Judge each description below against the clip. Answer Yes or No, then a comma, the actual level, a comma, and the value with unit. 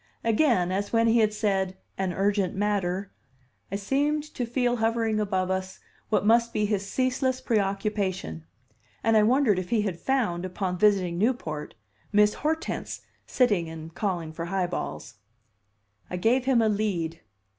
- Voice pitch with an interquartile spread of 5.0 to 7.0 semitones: No, average, 3.8 semitones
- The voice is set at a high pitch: Yes, high, 205 Hz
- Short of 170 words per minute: Yes, average, 155 wpm